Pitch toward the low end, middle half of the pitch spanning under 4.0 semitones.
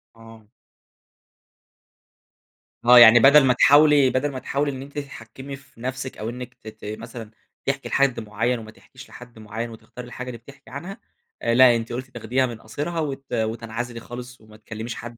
Yes: low, 120 Hz; average, 3.1 semitones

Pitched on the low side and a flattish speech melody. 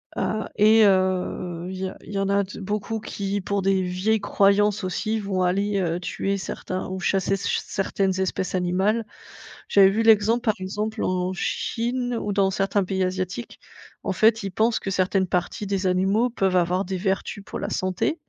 No: high, 195 Hz; narrow, 2.1 semitones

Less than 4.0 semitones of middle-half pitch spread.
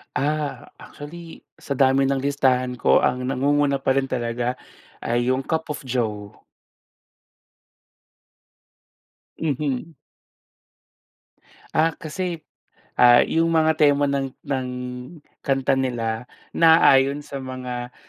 Yes: average, 2.7 semitones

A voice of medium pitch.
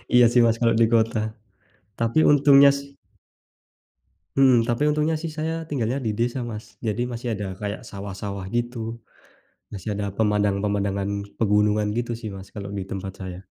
No: low, 110 Hz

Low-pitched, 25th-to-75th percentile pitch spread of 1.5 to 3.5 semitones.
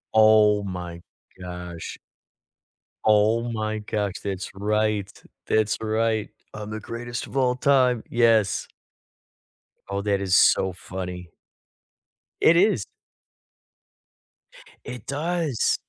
Yes: low, 110 Hz; average, 2.9 semitones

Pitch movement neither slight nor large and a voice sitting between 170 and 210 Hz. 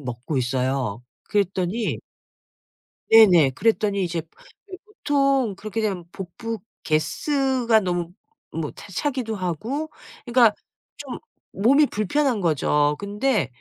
No: wide, 6.9 semitones; high, 205 Hz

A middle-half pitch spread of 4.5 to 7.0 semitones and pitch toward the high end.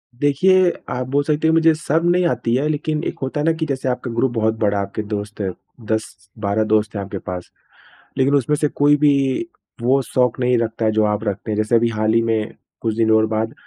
No: average, 4.9 semitones; low, 120 Hz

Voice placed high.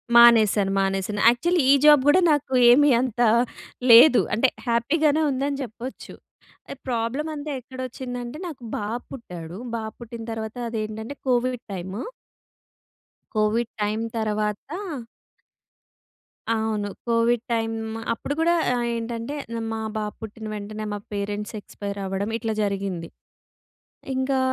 Yes: high, 230 Hz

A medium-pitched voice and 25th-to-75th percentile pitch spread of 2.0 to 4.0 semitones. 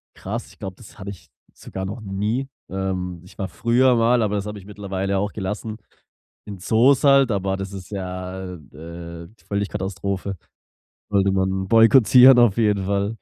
No: low, 100 Hz; narrow, 2.6 semitones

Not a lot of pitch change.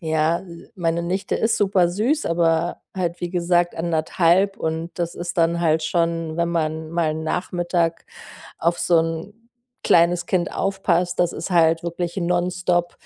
Yes: narrow, 1.3 semitones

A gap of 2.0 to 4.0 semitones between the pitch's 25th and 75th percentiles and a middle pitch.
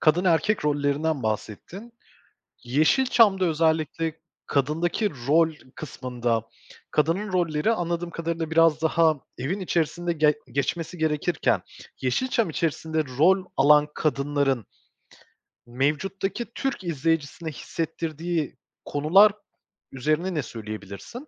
Yes: average, 3.2 semitones; medium, 160 Hz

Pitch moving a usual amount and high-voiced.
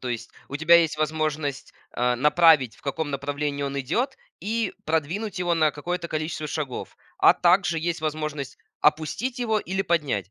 No: average, 3.3 semitones; medium, 155 Hz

